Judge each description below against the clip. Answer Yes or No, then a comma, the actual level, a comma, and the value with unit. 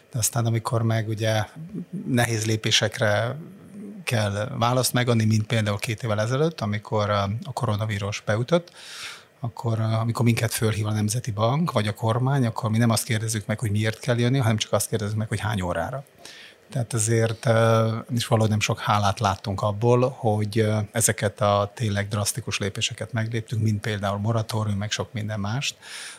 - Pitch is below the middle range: Yes, low, 110 Hz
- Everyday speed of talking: No, fast, 160 wpm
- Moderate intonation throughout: No, narrow, 2.0 semitones